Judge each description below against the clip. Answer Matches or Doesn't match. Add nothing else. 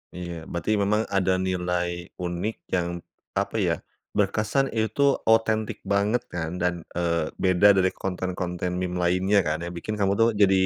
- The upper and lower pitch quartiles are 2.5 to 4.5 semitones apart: Matches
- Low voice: Matches